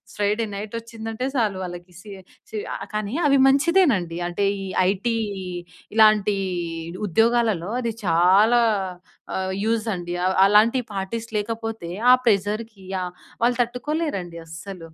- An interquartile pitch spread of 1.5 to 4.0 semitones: Yes, average, 3.5 semitones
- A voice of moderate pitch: No, high, 215 Hz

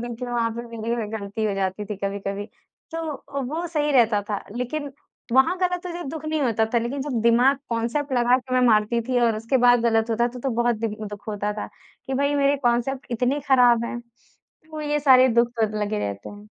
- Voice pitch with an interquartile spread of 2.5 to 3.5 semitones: No, average, 4.3 semitones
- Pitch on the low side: No, high, 240 Hz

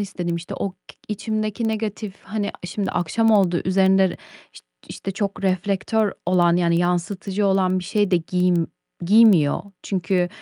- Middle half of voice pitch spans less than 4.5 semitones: Yes, average, 2.7 semitones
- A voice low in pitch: No, high, 190 Hz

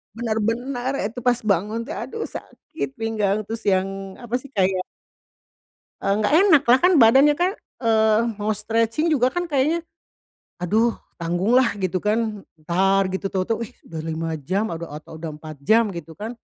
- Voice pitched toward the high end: Yes, high, 220 Hz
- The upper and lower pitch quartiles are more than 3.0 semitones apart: Yes, average, 4.2 semitones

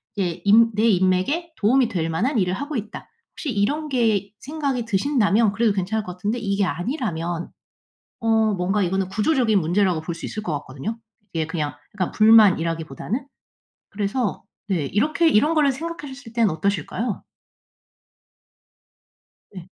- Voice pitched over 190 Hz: Yes, high, 210 Hz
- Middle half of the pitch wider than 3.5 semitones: Yes, average, 5.1 semitones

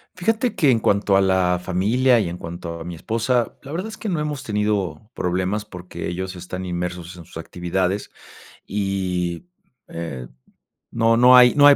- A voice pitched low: Yes, very low, 95 Hz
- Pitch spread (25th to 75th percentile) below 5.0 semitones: No, average, 5.3 semitones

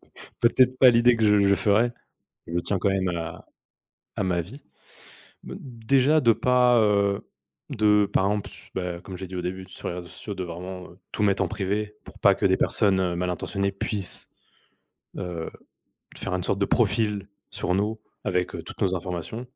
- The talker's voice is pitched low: Yes, low, 100 Hz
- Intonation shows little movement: No, average, 3.2 semitones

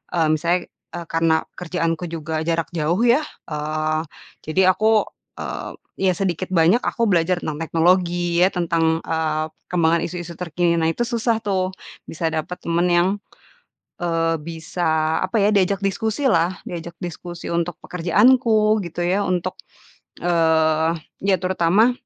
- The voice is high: No, medium, 175 Hz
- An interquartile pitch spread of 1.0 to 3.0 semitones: Yes, narrow, 2.4 semitones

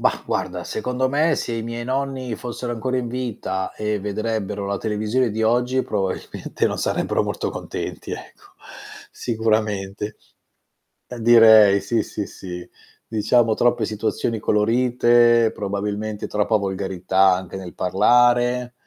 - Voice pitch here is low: Yes, low, 110 Hz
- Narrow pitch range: No, average, 3.0 semitones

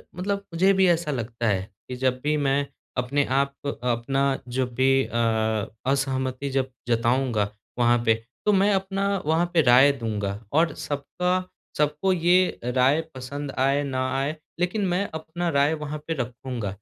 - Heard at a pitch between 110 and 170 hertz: Yes, medium, 140 Hz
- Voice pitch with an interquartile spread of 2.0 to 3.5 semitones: No, average, 4.6 semitones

